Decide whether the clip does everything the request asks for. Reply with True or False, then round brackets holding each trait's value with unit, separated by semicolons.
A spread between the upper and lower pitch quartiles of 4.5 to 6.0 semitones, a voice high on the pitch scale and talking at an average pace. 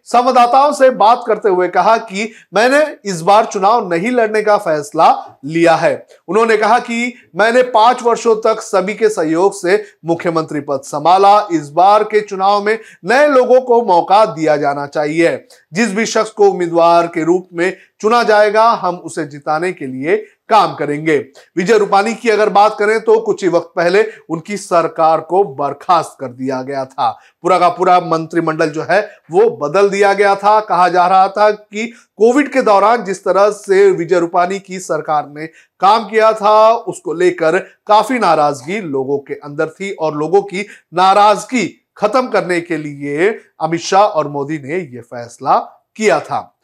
True (5.1 semitones; 195 Hz; 170 wpm)